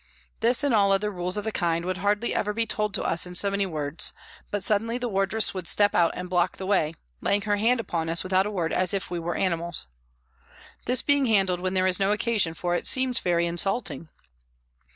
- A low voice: No, high, 195 Hz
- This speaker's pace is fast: Yes, fast, 225 wpm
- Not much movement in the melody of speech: No, average, 3.2 semitones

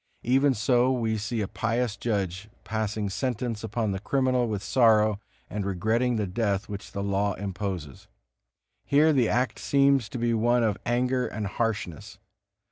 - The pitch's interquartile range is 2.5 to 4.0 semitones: Yes, average, 3.3 semitones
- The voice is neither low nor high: No, low, 110 Hz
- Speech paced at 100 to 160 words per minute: Yes, average, 155 wpm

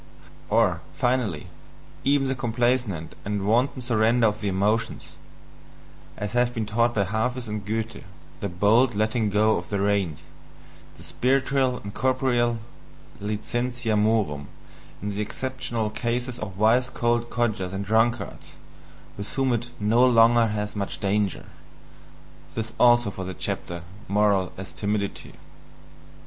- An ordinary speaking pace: No, slow, 130 wpm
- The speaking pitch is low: Yes, low, 110 Hz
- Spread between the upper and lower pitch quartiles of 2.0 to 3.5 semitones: Yes, average, 3.0 semitones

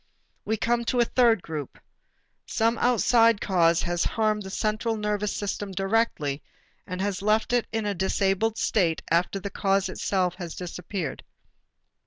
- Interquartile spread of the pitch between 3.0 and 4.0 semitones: Yes, average, 3.5 semitones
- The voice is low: No, high, 200 Hz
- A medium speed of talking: Yes, average, 150 wpm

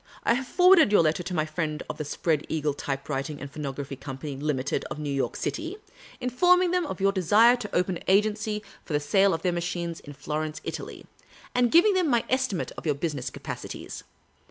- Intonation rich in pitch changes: Yes, wide, 7.9 semitones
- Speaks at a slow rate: No, fast, 205 wpm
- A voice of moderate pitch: Yes, medium, 170 Hz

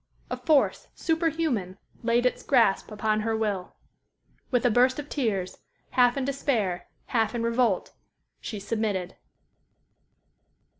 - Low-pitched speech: No, high, 230 Hz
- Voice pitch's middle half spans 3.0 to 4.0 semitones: Yes, average, 3.6 semitones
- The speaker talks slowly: Yes, slow, 120 wpm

